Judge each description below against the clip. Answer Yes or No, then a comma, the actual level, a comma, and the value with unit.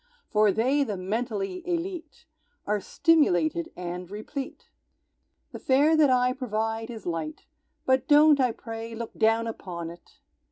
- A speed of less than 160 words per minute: Yes, slow, 135 wpm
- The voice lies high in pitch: Yes, high, 225 Hz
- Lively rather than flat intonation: Yes, wide, 5.7 semitones